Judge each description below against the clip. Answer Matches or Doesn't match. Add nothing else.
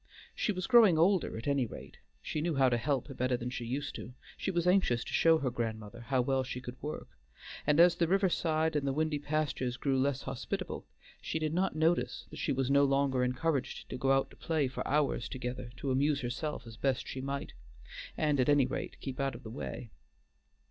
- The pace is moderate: Doesn't match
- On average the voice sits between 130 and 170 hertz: Matches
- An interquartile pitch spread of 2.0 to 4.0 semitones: Matches